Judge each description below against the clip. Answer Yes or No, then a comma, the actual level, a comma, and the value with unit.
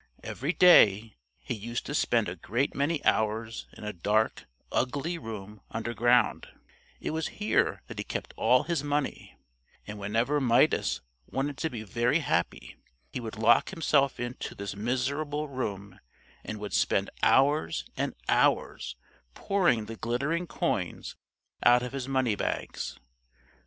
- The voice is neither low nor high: No, low, 120 Hz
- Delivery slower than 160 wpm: Yes, average, 140 wpm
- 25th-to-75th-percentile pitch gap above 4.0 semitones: Yes, average, 4.8 semitones